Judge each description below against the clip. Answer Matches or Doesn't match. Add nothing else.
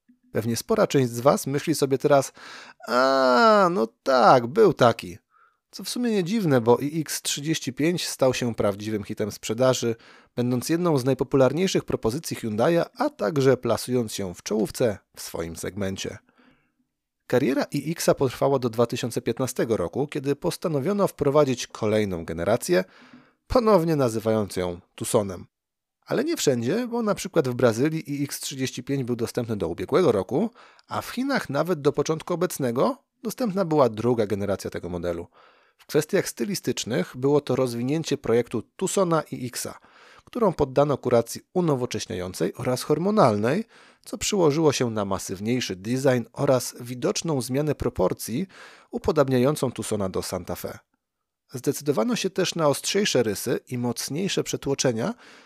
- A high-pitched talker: Doesn't match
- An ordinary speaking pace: Matches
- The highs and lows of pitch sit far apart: Matches